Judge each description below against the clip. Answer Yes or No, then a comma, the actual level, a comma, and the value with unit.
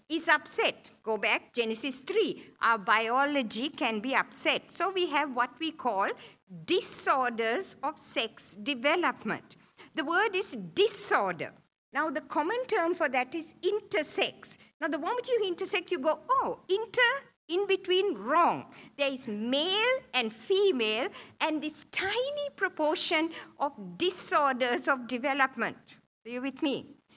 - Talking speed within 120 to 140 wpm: Yes, slow, 135 wpm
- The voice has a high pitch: Yes, very high, 305 Hz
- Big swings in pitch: Yes, wide, 6.6 semitones